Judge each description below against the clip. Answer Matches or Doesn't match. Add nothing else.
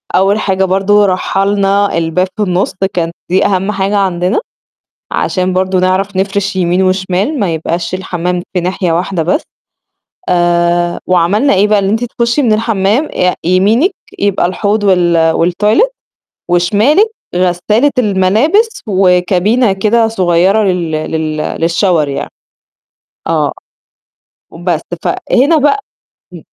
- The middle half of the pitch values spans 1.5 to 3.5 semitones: Matches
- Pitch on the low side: Doesn't match